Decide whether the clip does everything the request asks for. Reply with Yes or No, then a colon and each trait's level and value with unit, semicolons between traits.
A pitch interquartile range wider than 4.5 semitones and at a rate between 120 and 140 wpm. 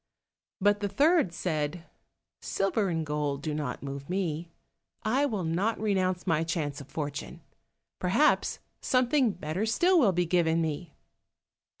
Yes: average, 5.1 semitones; slow, 135 wpm